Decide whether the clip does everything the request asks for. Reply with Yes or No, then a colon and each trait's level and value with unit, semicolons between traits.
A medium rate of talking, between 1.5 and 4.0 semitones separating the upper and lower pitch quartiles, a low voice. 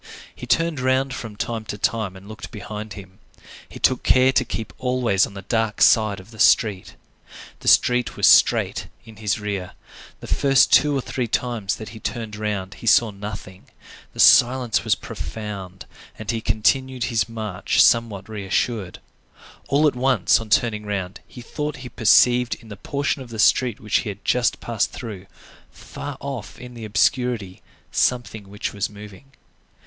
Yes: average, 175 wpm; average, 3.3 semitones; low, 110 Hz